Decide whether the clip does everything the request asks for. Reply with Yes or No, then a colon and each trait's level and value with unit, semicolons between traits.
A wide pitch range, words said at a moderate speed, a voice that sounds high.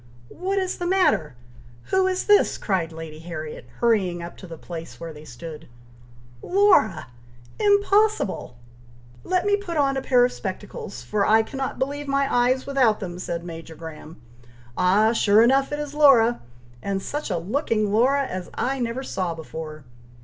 Yes: wide, 8.8 semitones; average, 165 wpm; high, 225 Hz